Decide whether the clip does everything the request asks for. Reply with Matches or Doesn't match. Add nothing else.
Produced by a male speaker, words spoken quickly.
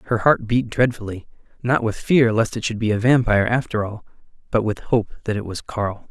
Matches